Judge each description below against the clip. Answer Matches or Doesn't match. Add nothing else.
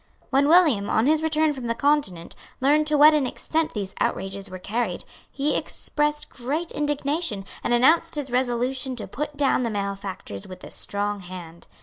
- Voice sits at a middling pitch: Doesn't match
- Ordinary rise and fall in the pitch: Doesn't match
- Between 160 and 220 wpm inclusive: Matches